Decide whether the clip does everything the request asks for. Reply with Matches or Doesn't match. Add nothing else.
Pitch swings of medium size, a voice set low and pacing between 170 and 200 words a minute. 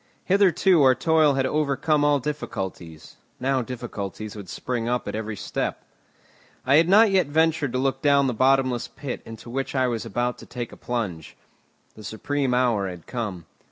Matches